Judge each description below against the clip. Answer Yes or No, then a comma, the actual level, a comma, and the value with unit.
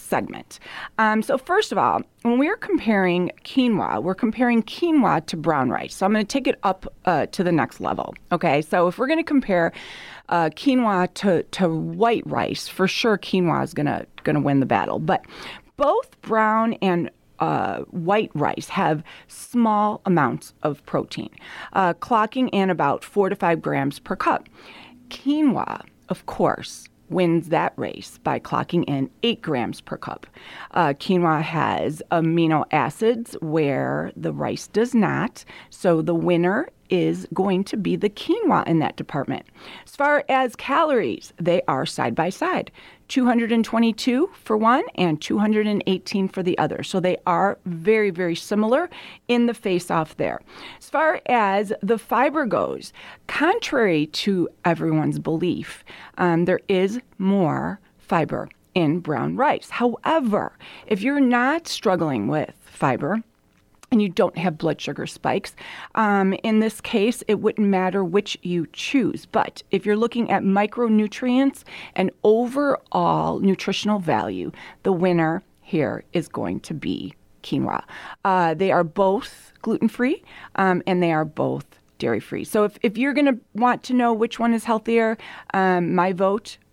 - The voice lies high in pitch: Yes, high, 205 Hz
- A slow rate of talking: No, average, 155 wpm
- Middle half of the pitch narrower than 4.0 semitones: No, average, 5.1 semitones